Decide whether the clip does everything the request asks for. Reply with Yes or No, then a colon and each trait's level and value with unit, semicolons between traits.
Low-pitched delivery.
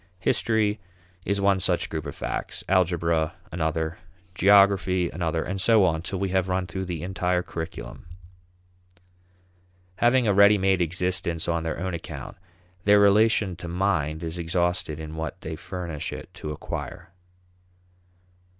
Yes: very low, 90 Hz